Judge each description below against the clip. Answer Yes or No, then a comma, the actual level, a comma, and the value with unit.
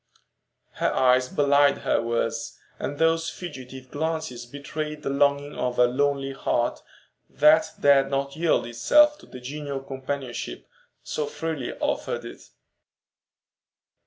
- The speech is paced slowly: Yes, slow, 125 wpm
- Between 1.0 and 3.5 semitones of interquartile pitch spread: Yes, average, 2.9 semitones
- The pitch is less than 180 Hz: Yes, medium, 140 Hz